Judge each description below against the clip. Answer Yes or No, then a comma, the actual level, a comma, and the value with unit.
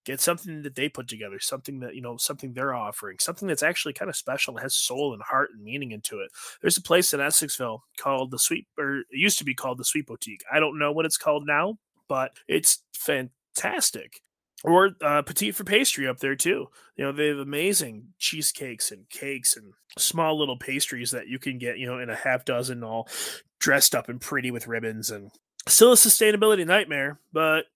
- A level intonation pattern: No, average, 4.1 semitones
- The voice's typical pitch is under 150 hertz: Yes, medium, 140 Hz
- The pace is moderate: No, fast, 210 wpm